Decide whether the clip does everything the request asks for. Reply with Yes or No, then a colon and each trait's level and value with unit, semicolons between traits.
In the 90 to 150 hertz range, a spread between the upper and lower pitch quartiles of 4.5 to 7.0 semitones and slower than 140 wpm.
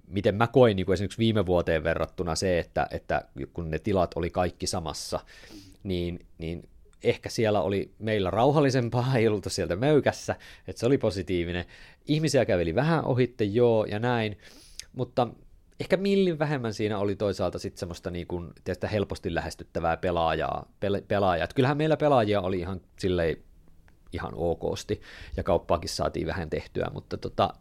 No: very low, 95 Hz; average, 5.1 semitones; average, 150 wpm